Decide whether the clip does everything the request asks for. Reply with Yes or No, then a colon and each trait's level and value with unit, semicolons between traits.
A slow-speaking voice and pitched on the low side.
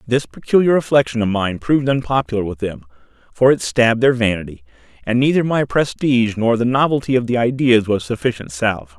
No: average, 180 wpm; low, 115 Hz